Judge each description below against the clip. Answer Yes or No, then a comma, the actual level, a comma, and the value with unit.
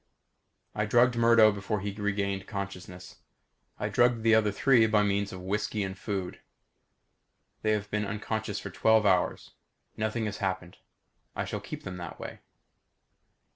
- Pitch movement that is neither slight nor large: No, narrow, 2.1 semitones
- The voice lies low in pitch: Yes, low, 105 Hz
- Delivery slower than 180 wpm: Yes, average, 150 wpm